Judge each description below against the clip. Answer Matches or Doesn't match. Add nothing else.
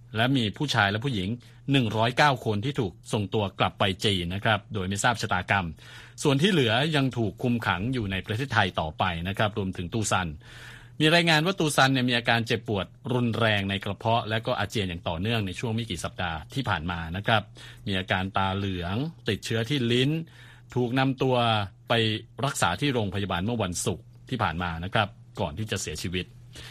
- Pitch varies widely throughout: Doesn't match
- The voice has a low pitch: Matches